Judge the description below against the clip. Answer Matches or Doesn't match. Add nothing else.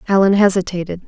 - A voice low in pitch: Doesn't match